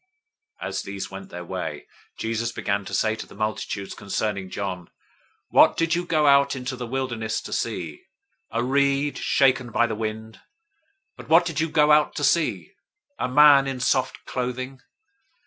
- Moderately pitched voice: No, low, 125 Hz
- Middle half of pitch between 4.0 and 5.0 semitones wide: Yes, average, 4.5 semitones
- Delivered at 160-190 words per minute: Yes, average, 175 wpm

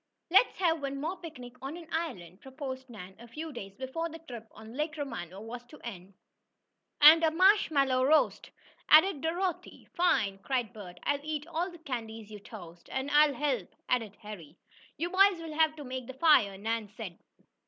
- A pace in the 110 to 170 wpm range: No, average, 180 wpm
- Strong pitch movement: Yes, wide, 6.4 semitones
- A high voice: Yes, very high, 265 Hz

